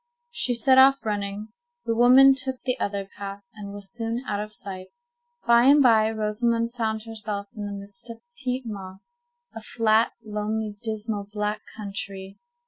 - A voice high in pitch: Yes, high, 220 Hz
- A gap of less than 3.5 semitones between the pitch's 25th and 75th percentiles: Yes, average, 2.8 semitones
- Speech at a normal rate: Yes, average, 160 wpm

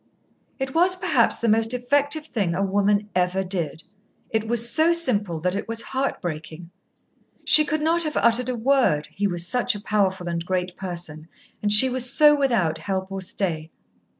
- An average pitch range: No, wide, 6.3 semitones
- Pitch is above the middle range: Yes, high, 205 Hz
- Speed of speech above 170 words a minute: Yes, average, 180 wpm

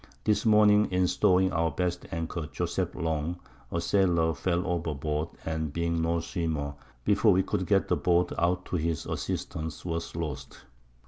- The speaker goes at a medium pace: Yes, average, 165 wpm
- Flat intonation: Yes, narrow, 2.0 semitones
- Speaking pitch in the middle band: No, very low, 85 Hz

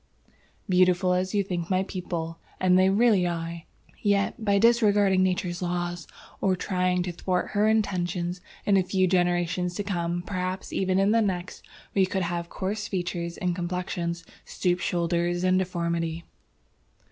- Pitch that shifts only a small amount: Yes, narrow, 1.7 semitones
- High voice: No, medium, 180 Hz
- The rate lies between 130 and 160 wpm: Yes, average, 155 wpm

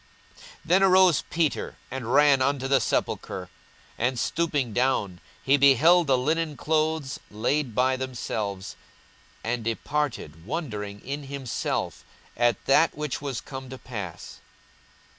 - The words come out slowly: Yes, slow, 125 wpm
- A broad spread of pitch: No, average, 4.2 semitones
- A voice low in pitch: Yes, low, 130 Hz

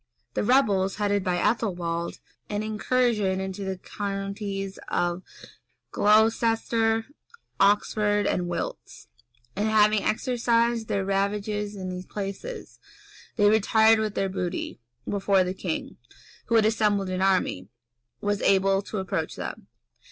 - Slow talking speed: Yes, slow, 125 wpm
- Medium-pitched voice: No, high, 205 Hz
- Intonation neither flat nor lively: No, narrow, 2.2 semitones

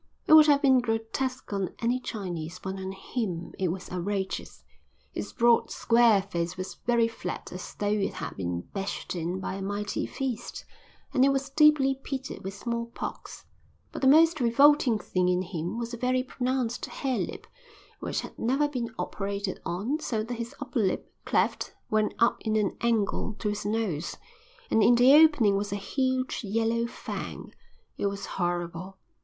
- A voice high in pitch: Yes, high, 225 Hz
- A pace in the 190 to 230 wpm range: No, average, 170 wpm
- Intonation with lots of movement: No, average, 4.8 semitones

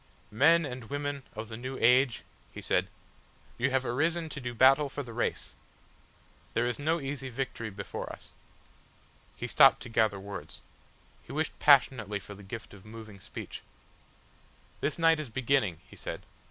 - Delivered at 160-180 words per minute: Yes, average, 165 wpm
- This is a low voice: Yes, low, 125 Hz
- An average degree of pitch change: Yes, average, 4.3 semitones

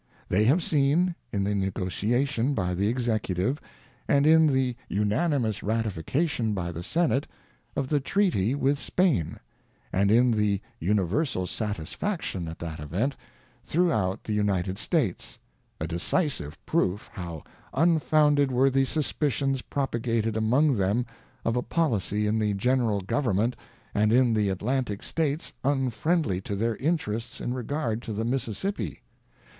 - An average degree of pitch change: No, wide, 5.9 semitones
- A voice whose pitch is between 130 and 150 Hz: No, low, 115 Hz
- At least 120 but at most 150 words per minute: Yes, average, 140 wpm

